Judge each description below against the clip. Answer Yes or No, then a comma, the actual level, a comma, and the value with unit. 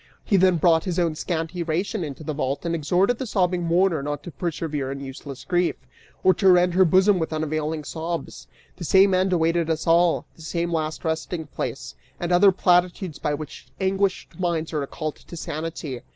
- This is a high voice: No, medium, 170 Hz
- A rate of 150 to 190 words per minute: Yes, average, 185 wpm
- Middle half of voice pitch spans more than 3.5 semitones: No, narrow, 2.6 semitones